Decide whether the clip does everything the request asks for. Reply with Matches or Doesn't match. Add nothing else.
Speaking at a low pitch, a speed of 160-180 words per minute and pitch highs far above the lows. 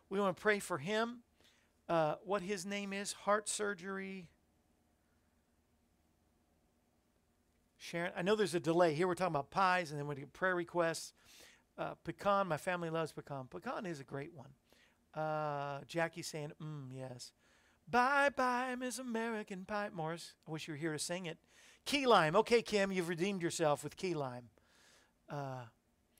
Doesn't match